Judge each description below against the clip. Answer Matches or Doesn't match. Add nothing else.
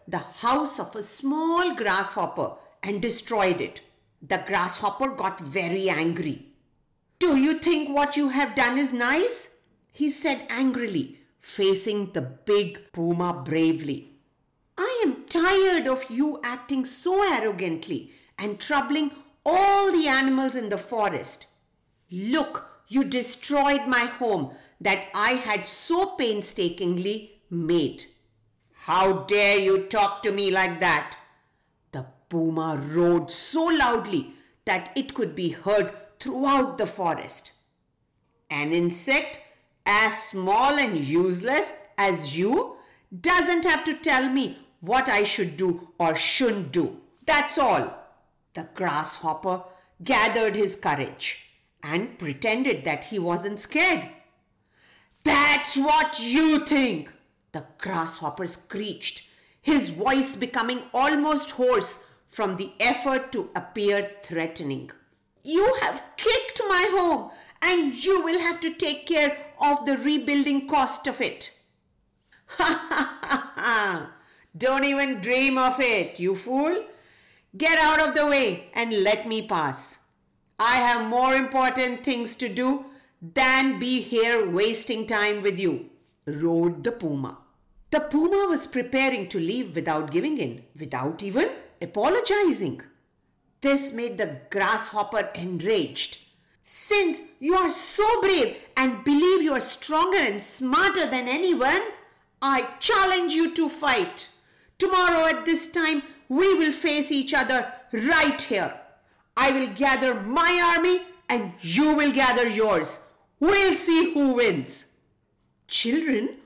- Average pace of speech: Doesn't match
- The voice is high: Matches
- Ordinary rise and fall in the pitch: Doesn't match